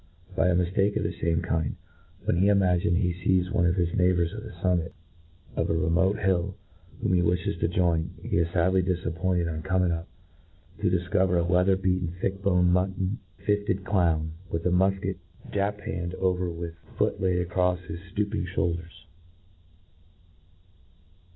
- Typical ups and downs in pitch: No, narrow, 1.7 semitones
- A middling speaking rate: Yes, average, 165 wpm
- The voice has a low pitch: Yes, very low, 90 Hz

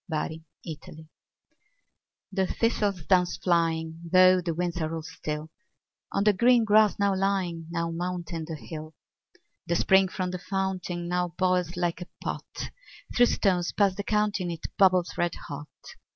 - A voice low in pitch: No, medium, 180 Hz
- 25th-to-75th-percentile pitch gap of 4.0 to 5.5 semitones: No, narrow, 2.6 semitones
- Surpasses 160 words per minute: No, average, 150 wpm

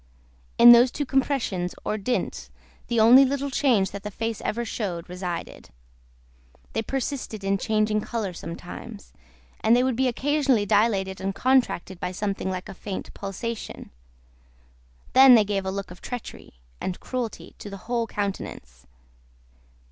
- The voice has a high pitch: Yes, high, 215 Hz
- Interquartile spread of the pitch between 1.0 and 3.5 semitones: No, average, 4.3 semitones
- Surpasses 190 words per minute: No, average, 150 wpm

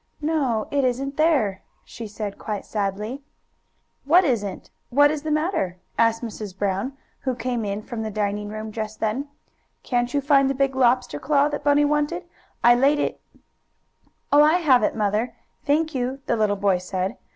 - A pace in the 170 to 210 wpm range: Yes, average, 175 wpm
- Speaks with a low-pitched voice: No, high, 245 Hz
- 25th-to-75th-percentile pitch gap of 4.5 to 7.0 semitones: Yes, average, 5.3 semitones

